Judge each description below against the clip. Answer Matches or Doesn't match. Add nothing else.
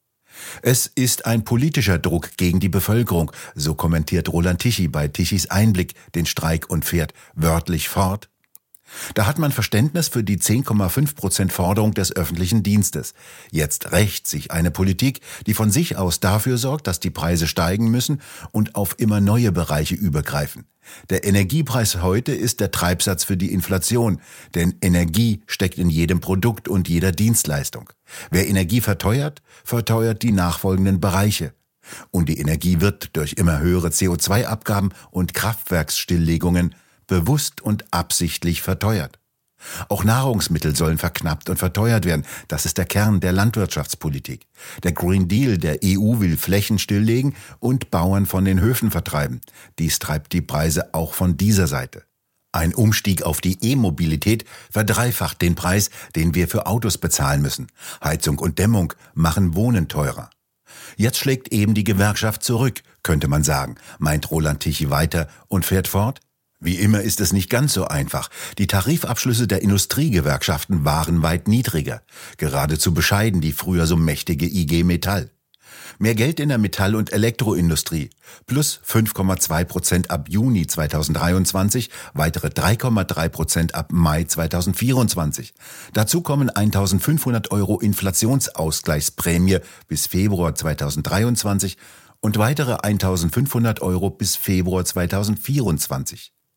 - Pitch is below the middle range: Matches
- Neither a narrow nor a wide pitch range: Matches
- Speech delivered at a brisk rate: Doesn't match